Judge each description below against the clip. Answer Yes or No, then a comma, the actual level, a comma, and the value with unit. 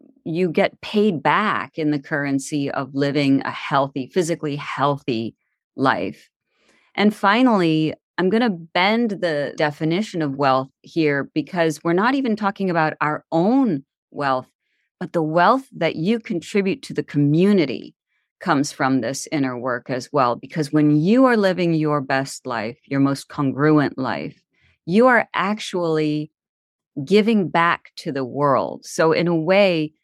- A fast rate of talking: No, average, 150 wpm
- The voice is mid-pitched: Yes, medium, 155 Hz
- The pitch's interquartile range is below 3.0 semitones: No, average, 5.2 semitones